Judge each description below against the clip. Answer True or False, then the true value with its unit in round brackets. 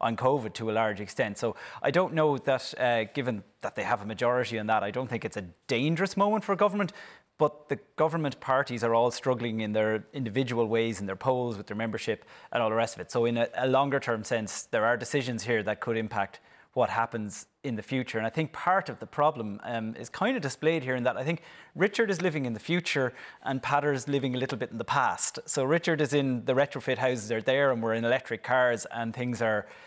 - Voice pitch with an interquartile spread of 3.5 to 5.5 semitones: True (3.9 semitones)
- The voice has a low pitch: True (125 Hz)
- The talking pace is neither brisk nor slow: False (245 wpm)